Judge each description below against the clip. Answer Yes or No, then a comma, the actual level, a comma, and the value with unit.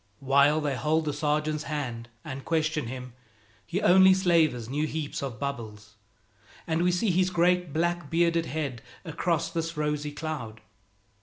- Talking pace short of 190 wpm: Yes, average, 150 wpm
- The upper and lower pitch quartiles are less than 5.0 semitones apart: Yes, average, 3.4 semitones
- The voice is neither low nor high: Yes, medium, 155 Hz